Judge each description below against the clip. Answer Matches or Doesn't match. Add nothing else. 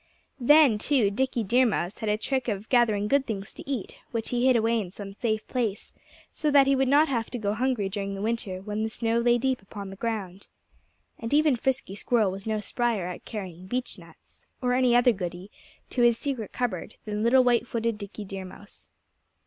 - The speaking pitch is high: Matches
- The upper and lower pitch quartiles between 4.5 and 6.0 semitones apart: Doesn't match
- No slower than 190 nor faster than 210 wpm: Matches